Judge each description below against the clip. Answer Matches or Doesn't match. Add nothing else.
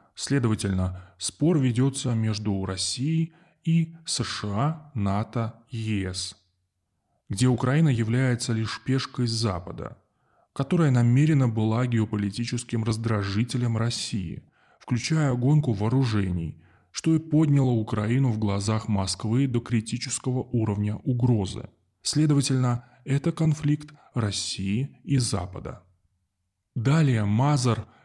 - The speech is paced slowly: Matches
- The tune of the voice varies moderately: Matches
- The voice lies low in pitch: Matches